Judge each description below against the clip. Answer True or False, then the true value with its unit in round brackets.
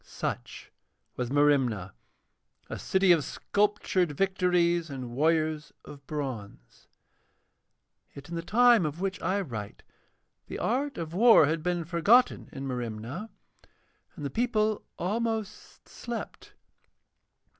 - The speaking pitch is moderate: True (170 Hz)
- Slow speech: True (115 wpm)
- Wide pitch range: True (6.6 semitones)